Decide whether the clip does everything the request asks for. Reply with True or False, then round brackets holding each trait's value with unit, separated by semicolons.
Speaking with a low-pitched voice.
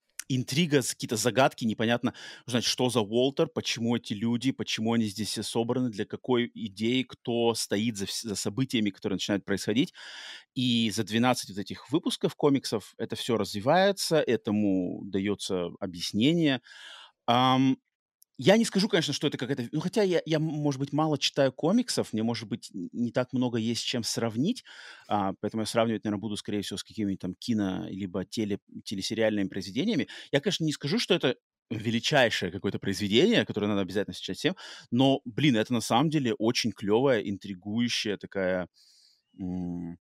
True (115 Hz)